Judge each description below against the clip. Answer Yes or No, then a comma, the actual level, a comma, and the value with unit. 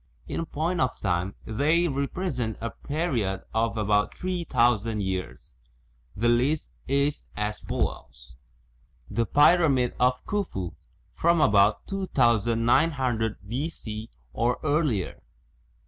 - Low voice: Yes, low, 120 Hz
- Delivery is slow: Yes, slow, 105 wpm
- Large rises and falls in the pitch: Yes, wide, 6.2 semitones